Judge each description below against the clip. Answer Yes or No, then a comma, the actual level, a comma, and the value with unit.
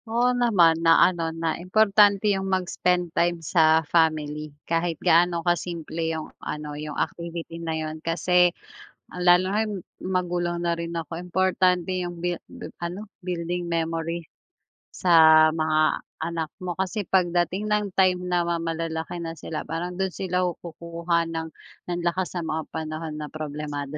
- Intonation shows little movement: Yes, narrow, 1.9 semitones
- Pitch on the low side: No, medium, 170 Hz